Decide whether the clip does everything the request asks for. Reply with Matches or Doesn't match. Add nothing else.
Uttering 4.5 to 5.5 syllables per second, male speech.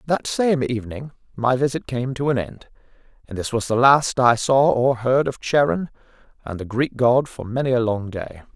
Matches